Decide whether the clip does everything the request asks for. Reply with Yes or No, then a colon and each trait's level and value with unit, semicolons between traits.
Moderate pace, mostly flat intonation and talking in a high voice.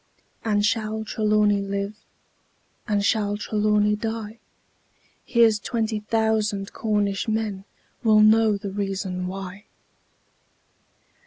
No: slow, 95 wpm; narrow, 1.5 semitones; high, 210 Hz